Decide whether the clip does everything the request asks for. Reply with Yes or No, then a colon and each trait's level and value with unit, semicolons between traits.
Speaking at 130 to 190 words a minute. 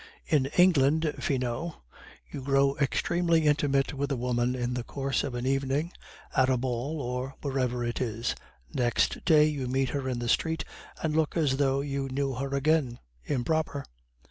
Yes: average, 170 wpm